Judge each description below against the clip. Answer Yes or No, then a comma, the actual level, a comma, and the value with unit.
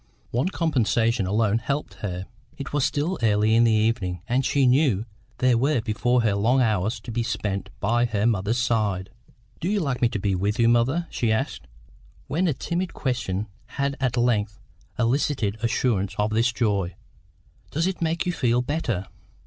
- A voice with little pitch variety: No, average, 4.1 semitones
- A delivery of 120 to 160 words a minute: No, average, 175 wpm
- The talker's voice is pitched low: Yes, low, 115 Hz